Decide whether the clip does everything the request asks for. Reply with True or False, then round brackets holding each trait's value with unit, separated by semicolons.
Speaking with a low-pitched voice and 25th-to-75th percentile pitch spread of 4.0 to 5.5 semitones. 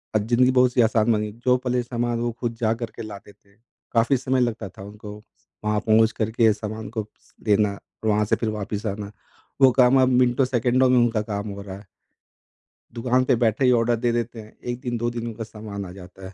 False (115 Hz; 2.5 semitones)